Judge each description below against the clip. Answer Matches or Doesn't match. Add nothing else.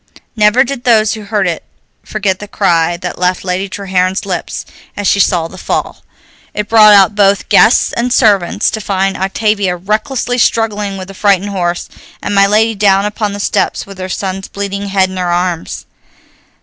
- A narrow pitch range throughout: Matches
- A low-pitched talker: Doesn't match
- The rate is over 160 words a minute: Matches